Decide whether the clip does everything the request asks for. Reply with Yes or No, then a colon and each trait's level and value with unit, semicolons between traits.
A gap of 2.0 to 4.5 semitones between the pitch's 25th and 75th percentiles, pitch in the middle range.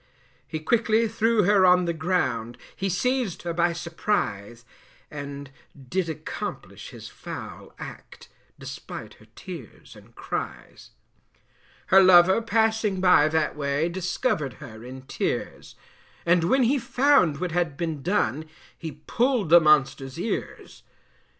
No: wide, 5.5 semitones; medium, 175 Hz